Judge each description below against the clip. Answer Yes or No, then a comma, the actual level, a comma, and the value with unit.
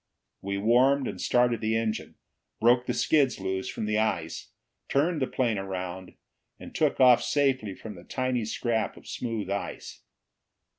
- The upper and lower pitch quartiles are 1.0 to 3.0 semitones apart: No, average, 4.5 semitones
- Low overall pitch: Yes, low, 115 Hz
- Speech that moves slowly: No, average, 155 wpm